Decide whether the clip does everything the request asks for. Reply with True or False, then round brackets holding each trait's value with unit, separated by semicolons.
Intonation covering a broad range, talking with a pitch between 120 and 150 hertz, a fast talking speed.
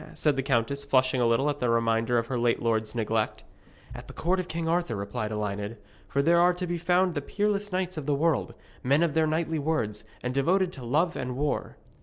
True (6.4 semitones; 140 Hz; 225 wpm)